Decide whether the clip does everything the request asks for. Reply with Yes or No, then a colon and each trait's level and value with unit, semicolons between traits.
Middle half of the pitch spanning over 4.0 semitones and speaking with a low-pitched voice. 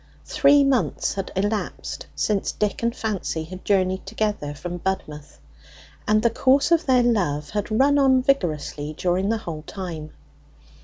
No: wide, 5.6 semitones; high, 205 Hz